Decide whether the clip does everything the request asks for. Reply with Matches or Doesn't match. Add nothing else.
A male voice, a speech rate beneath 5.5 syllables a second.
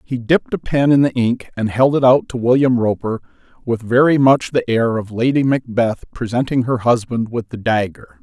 Matches